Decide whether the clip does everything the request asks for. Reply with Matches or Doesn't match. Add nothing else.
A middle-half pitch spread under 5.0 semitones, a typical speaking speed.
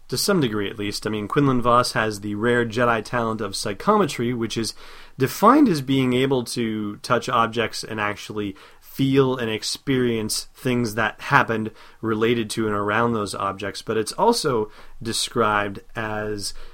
Matches